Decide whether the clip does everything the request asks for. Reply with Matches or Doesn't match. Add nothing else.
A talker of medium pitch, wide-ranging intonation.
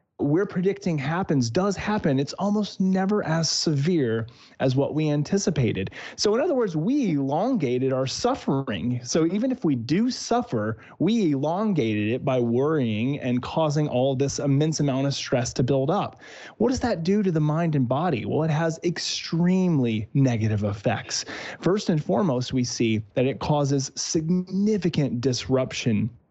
Matches